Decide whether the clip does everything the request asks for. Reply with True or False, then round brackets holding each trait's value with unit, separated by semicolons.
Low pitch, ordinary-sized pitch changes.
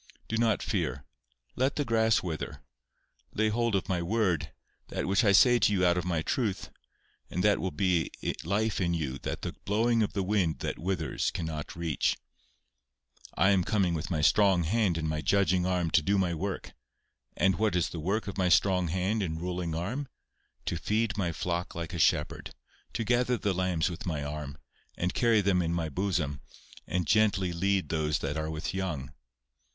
True (90 Hz; 3.8 semitones)